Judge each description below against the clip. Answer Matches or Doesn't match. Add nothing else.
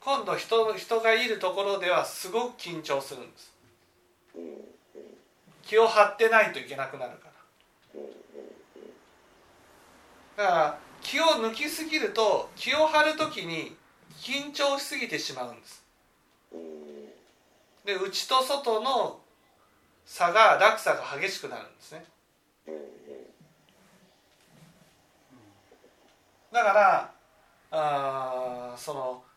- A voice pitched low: Doesn't match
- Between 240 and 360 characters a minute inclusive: Doesn't match